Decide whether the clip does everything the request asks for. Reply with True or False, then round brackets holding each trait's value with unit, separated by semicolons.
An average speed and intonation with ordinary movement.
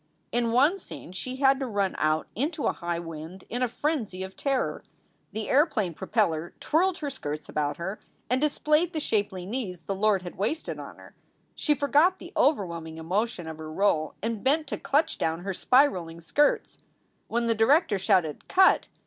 False (180 wpm; 8.4 semitones)